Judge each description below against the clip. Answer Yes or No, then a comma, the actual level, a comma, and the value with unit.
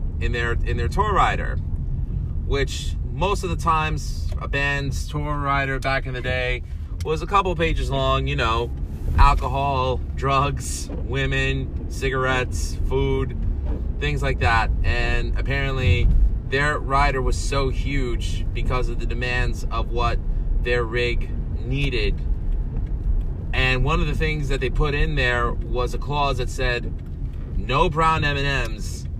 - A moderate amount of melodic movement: No, wide, 8.9 semitones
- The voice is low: Yes, low, 105 Hz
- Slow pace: No, average, 145 wpm